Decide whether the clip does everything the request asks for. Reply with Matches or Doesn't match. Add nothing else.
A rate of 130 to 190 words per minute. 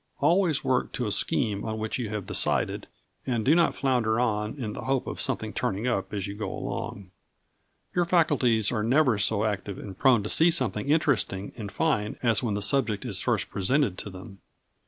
Doesn't match